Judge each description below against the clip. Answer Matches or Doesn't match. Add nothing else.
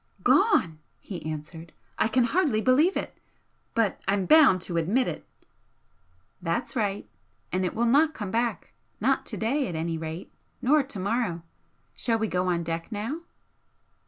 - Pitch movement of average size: Doesn't match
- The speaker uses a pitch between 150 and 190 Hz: Doesn't match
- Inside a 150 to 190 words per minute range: Matches